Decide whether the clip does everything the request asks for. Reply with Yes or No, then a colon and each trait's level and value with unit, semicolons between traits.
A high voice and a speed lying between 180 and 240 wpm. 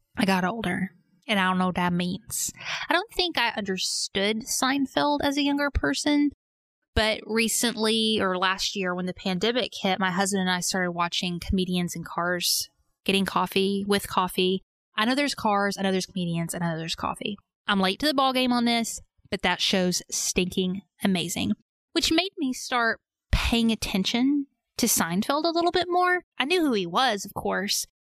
Yes: high, 205 Hz; average, 185 wpm